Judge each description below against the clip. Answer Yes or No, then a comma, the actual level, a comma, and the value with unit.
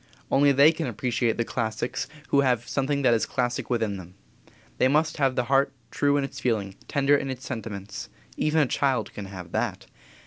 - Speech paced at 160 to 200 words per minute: Yes, average, 195 wpm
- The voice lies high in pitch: No, low, 130 Hz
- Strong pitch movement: No, average, 3.9 semitones